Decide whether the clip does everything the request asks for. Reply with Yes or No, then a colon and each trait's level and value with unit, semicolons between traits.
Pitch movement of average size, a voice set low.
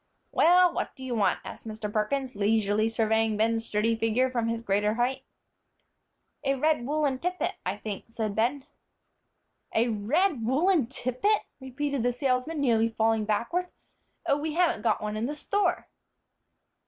No: average, 4.5 semitones; high, 240 Hz